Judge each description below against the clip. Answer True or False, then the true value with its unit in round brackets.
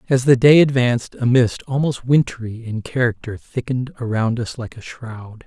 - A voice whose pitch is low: True (120 Hz)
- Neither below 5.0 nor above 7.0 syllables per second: False (4.8 syllables/s)